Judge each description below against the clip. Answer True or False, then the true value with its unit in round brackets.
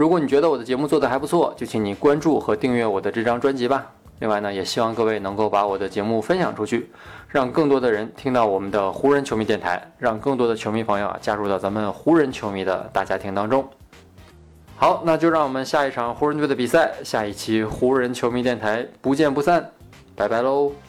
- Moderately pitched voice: False (115 Hz)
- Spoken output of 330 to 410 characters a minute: True (340 characters per minute)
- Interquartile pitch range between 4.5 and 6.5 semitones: True (5.0 semitones)